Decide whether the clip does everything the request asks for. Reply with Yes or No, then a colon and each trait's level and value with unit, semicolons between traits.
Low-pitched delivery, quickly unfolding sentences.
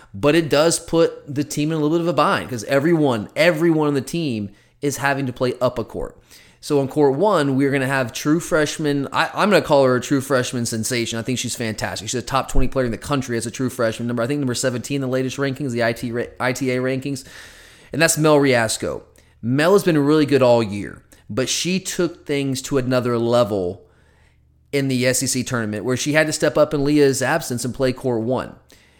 Yes: low, 130 Hz; fast, 230 wpm